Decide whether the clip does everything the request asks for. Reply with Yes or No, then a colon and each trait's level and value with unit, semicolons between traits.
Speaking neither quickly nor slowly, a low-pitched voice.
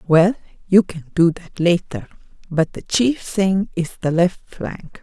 No: average, 165 wpm; medium, 180 Hz